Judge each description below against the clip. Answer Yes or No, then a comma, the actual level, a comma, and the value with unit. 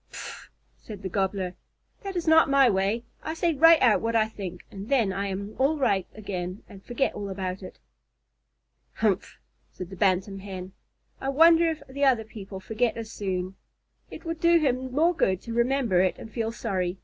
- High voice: Yes, high, 220 Hz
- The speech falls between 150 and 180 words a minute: No, average, 190 wpm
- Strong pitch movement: Yes, wide, 6.1 semitones